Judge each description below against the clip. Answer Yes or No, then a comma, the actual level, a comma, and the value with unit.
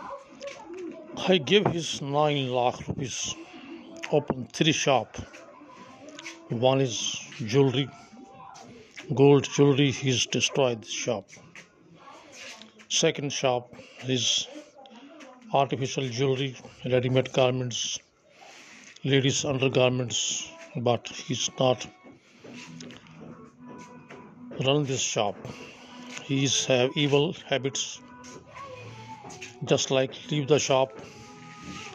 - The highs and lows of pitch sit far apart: No, average, 4.4 semitones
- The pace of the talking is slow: Yes, slow, 85 wpm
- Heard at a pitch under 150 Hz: Yes, low, 135 Hz